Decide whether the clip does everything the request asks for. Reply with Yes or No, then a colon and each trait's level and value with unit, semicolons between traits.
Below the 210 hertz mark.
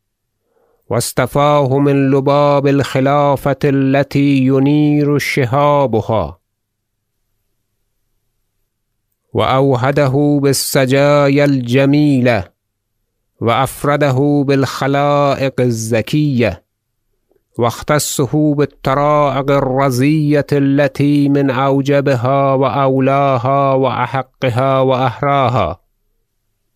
Yes: low, 135 Hz